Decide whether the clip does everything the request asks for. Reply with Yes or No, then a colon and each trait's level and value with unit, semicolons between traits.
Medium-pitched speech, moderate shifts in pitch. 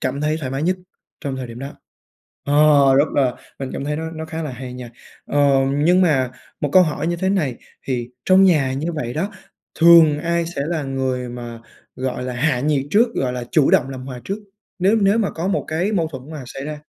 Yes: medium, 145 Hz; average, 4.2 semitones